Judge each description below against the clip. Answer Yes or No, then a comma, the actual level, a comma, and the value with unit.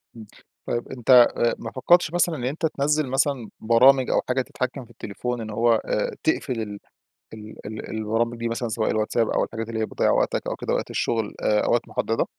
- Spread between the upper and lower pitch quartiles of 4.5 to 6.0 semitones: No, average, 2.7 semitones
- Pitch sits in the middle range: No, low, 120 Hz